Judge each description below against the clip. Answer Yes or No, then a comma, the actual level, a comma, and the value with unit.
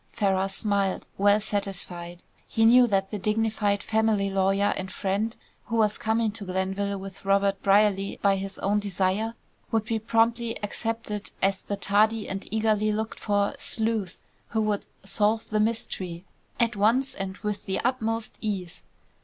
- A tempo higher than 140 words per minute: Yes, average, 155 wpm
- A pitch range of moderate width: No, narrow, 2.2 semitones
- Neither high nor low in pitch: No, high, 205 Hz